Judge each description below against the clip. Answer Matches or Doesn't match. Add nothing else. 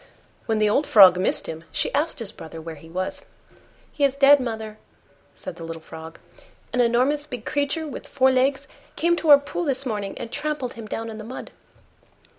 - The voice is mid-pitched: Doesn't match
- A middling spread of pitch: Doesn't match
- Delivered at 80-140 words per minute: Doesn't match